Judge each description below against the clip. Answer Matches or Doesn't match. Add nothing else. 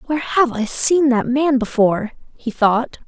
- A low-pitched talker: Doesn't match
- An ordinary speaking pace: Matches